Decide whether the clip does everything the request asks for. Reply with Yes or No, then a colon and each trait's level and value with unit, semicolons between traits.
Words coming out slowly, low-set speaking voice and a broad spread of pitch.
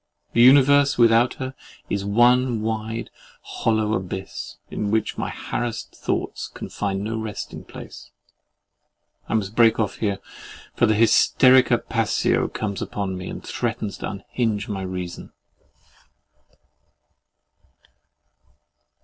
No: slow, 115 wpm; low, 110 Hz; average, 2.9 semitones